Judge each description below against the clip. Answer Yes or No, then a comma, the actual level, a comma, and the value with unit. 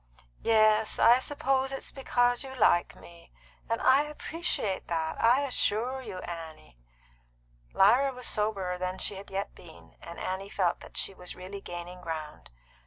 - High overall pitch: Yes, high, 200 Hz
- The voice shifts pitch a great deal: Yes, wide, 5.9 semitones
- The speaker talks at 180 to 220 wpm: No, average, 155 wpm